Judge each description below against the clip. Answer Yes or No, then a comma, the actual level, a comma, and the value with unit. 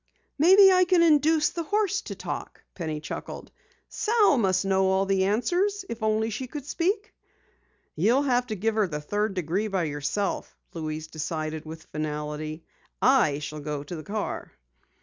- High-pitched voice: Yes, high, 205 Hz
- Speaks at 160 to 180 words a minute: Yes, average, 165 wpm